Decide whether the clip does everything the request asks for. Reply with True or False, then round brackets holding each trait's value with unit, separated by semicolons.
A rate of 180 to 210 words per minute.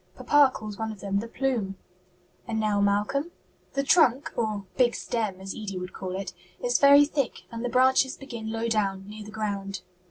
True (190 wpm)